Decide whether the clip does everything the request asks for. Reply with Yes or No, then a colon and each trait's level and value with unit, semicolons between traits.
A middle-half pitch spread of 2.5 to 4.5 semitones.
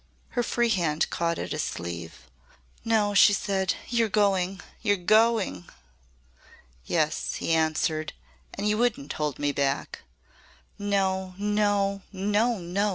Yes: average, 4.2 semitones